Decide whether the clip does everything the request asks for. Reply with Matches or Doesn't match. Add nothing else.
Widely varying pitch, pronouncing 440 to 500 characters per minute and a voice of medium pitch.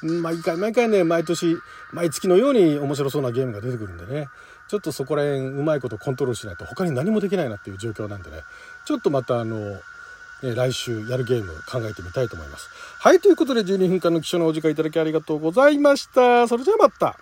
Matches